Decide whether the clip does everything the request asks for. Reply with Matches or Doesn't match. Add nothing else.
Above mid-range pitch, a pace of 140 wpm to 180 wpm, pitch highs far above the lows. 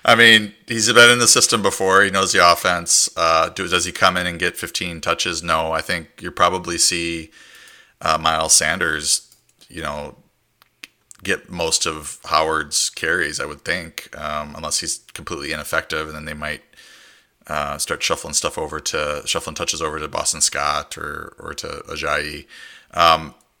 Doesn't match